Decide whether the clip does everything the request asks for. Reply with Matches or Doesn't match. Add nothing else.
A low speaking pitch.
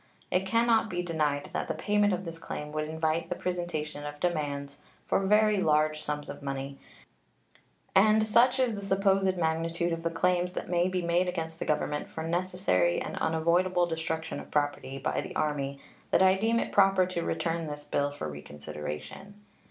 Doesn't match